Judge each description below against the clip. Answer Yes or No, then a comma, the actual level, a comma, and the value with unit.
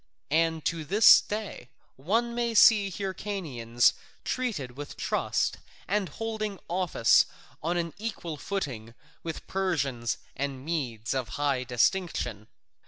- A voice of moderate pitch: Yes, medium, 165 Hz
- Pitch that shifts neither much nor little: No, wide, 7.5 semitones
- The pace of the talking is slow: Yes, slow, 115 wpm